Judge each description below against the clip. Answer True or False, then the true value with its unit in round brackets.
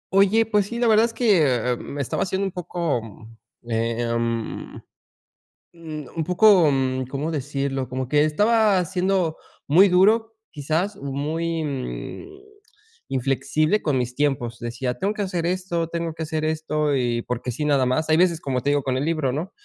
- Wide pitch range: True (5.7 semitones)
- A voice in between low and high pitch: True (155 Hz)